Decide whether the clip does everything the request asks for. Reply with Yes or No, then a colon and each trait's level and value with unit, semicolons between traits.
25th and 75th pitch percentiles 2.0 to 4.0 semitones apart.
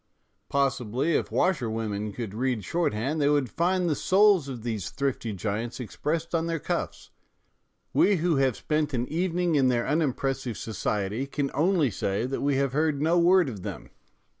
No: wide, 5.6 semitones